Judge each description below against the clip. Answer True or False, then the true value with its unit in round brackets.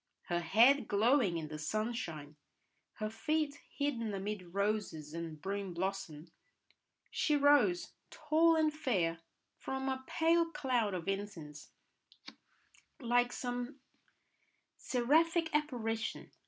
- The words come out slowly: True (110 wpm)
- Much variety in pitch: True (7.8 semitones)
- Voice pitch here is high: True (225 Hz)